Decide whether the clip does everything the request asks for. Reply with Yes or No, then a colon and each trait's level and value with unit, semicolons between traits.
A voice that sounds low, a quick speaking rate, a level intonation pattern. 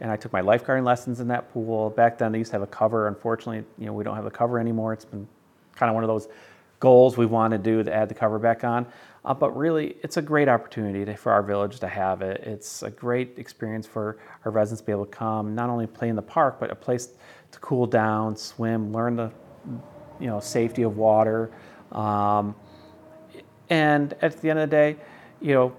Yes: low, 115 Hz; fast, 235 wpm; narrow, 2.3 semitones